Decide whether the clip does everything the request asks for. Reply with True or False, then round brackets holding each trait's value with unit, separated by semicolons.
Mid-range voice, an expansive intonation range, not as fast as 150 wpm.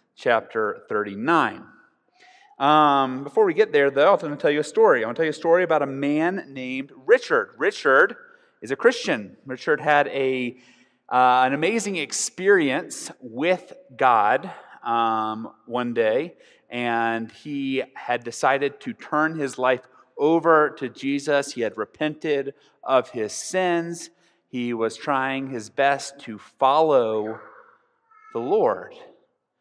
True (145 Hz; 8.5 semitones; 140 wpm)